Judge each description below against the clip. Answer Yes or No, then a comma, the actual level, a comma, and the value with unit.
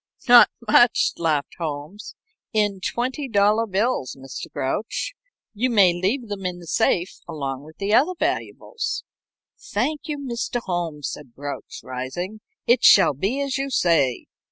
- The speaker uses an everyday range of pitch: No, wide, 7.5 semitones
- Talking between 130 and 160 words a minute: Yes, average, 145 wpm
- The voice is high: Yes, high, 200 Hz